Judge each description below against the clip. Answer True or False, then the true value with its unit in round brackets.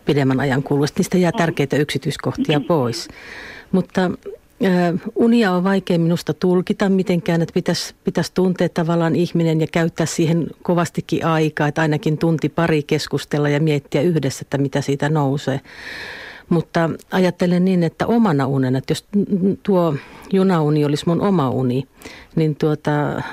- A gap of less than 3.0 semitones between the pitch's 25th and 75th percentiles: False (3.6 semitones)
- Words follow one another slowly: False (140 wpm)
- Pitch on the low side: False (165 Hz)